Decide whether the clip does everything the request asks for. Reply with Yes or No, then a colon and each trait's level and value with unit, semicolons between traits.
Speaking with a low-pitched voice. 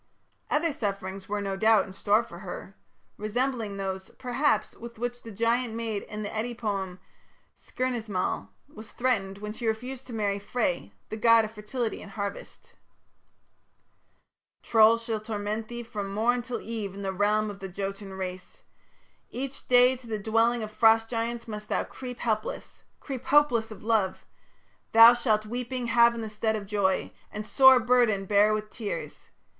No: high, 220 Hz